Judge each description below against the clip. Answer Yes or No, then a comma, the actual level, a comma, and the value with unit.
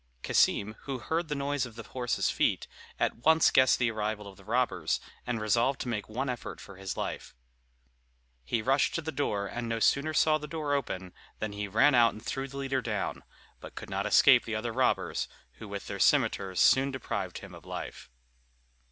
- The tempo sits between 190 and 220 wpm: Yes, average, 200 wpm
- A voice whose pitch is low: Yes, low, 120 Hz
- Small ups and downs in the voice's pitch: No, average, 4.7 semitones